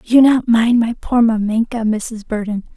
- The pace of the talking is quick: No, average, 175 wpm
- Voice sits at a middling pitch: No, high, 225 Hz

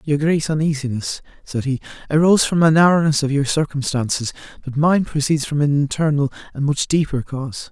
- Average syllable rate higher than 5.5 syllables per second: Yes, 5.8 syllables/s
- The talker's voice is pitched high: No, medium, 145 Hz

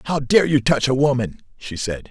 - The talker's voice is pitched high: No, low, 135 Hz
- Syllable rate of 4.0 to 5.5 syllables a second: Yes, 5.2 syllables/s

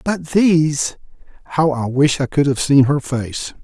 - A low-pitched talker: No, medium, 145 Hz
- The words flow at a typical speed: Yes, average, 180 wpm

